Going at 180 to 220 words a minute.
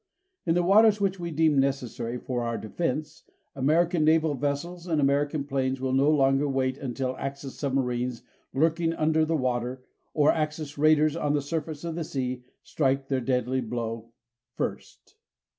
No: average, 160 wpm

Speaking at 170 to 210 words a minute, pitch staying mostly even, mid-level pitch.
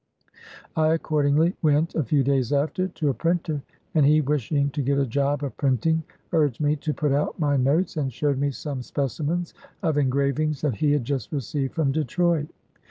Yes: average, 185 wpm; narrow, 2.1 semitones; medium, 145 Hz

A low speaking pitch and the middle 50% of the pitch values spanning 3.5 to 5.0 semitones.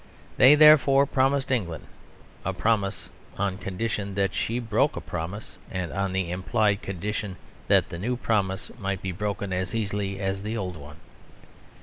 No: low, 100 Hz; average, 3.1 semitones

